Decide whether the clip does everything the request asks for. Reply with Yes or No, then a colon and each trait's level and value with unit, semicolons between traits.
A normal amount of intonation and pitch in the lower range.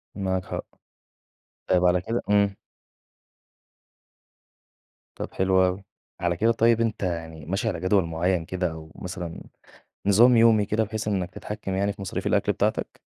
Yes: average, 3.0 semitones; very low, 95 Hz